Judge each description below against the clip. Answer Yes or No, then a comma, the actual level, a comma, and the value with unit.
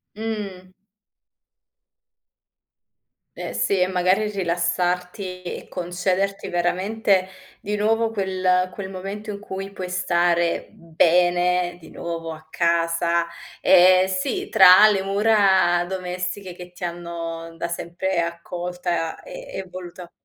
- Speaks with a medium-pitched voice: Yes, medium, 180 Hz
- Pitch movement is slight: Yes, narrow, 1.9 semitones